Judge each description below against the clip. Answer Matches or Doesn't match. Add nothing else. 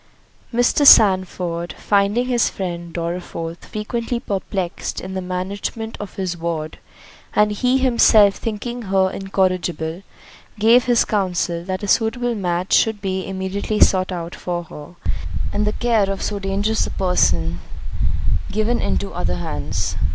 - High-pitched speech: Matches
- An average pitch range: Matches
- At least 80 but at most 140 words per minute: Matches